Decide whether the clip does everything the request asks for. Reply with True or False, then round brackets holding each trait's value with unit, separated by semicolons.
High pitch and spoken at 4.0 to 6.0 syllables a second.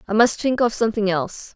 False (220 Hz; 6.5 syllables/s)